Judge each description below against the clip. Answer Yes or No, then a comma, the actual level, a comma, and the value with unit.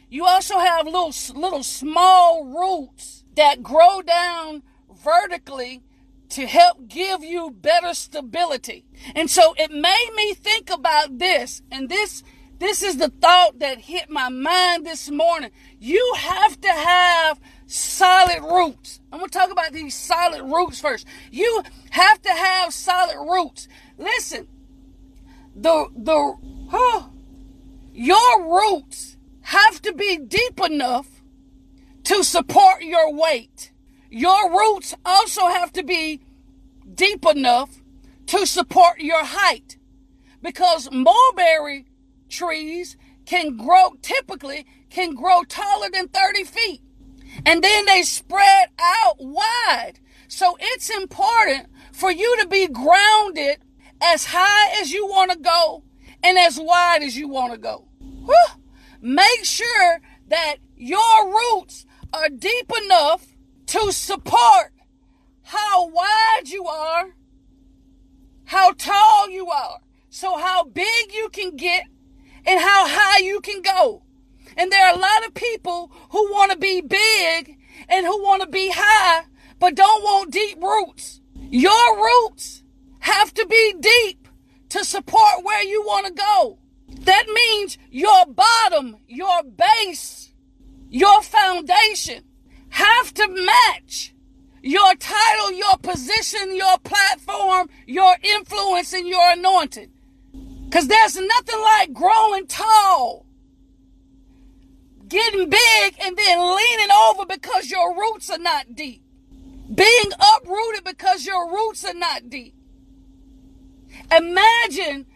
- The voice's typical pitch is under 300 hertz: No, very high, 360 Hz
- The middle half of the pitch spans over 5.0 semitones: Yes, wide, 5.5 semitones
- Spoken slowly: Yes, slow, 125 wpm